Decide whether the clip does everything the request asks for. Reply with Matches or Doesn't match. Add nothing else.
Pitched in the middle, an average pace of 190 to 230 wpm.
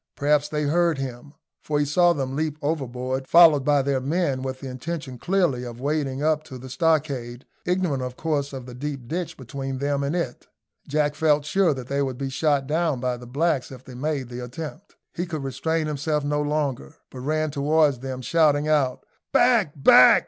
Matches